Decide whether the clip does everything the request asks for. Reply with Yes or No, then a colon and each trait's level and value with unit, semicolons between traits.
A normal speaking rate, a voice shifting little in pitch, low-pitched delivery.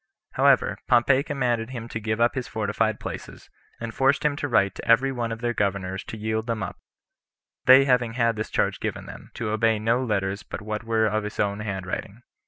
No: fast, 210 wpm; narrow, 2.3 semitones; low, 115 Hz